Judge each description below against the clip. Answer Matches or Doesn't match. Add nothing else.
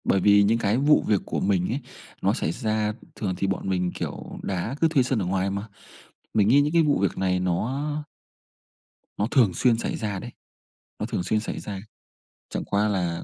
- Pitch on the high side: Doesn't match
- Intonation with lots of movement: Doesn't match